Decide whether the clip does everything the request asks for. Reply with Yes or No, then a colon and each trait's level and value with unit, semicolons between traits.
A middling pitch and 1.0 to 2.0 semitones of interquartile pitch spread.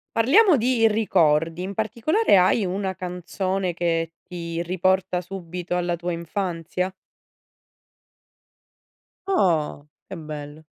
No: medium, 180 Hz; average, 2.8 semitones